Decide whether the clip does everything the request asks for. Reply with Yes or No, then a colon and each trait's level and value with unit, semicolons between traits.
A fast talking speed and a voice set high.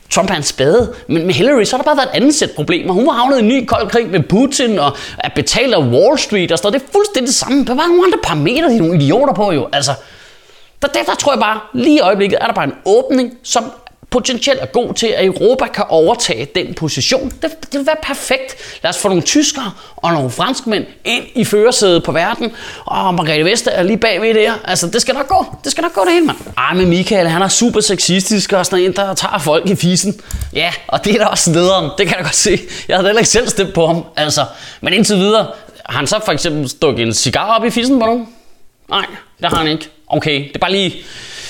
Yes: fast, 255 wpm; high, 215 Hz